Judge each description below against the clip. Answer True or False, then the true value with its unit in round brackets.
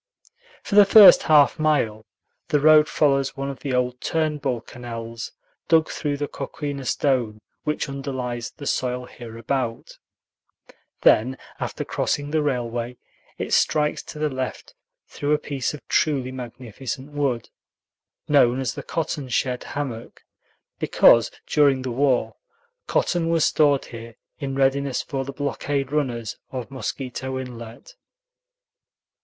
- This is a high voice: False (135 Hz)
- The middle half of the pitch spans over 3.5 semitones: False (2.9 semitones)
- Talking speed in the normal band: False (130 wpm)